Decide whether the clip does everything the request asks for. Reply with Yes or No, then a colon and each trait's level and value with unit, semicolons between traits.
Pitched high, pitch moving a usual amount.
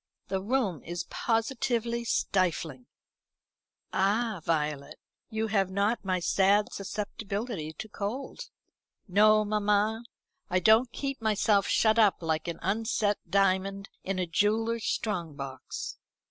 Yes: high, 205 Hz; average, 3.1 semitones